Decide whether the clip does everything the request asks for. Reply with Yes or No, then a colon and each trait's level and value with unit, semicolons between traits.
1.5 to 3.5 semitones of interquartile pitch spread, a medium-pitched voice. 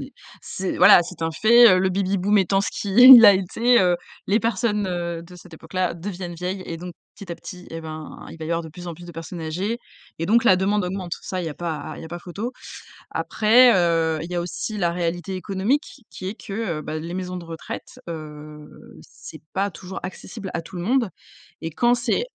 Yes: average, 3.2 semitones; medium, 180 Hz